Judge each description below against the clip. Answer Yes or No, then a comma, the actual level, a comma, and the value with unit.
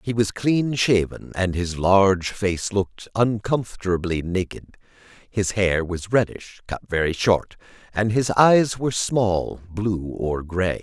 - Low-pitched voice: Yes, low, 100 Hz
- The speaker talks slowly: No, average, 145 wpm